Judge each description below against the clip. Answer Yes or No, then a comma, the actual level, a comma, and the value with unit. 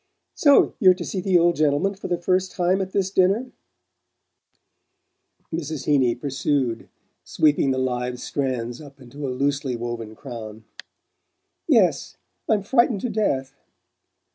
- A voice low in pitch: No, medium, 145 Hz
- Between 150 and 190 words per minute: No, slow, 135 wpm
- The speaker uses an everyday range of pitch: No, wide, 6.6 semitones